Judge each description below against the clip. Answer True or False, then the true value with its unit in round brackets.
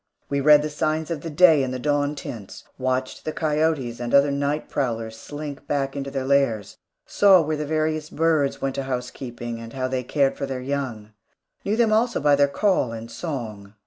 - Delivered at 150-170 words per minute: False (200 wpm)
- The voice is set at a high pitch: False (140 Hz)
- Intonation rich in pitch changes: False (3.2 semitones)